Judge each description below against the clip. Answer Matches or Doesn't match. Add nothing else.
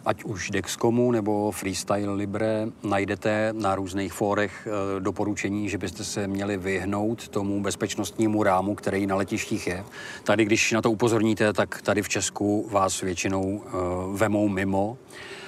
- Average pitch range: Doesn't match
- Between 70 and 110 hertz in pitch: Matches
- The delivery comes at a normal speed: Matches